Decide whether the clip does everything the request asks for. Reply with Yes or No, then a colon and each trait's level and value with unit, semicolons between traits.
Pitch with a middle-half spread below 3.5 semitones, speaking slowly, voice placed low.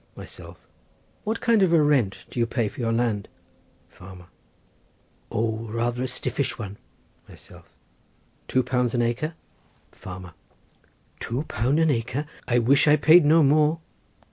No: average, 4.7 semitones; slow, 125 wpm; low, 125 Hz